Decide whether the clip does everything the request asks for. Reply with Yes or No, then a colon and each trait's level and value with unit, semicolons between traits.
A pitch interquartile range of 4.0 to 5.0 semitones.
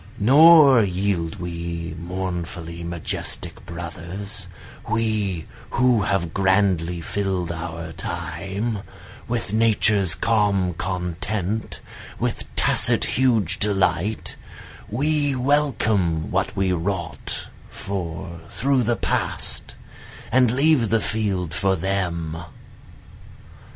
Yes: average, 4.5 semitones